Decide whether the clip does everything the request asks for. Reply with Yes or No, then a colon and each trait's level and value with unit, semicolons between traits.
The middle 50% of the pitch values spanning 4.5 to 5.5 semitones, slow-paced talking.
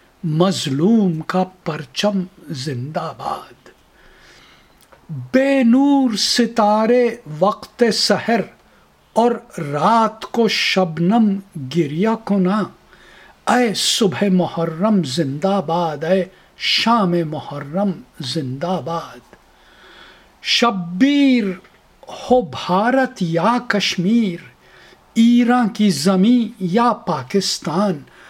Yes: average, 5.2 semitones; slow, 75 wpm